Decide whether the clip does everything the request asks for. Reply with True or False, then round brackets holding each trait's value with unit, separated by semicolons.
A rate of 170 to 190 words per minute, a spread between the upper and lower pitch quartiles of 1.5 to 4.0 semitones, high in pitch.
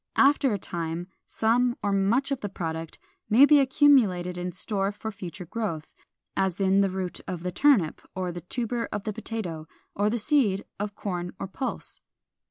False (180 wpm; 4.5 semitones; 200 Hz)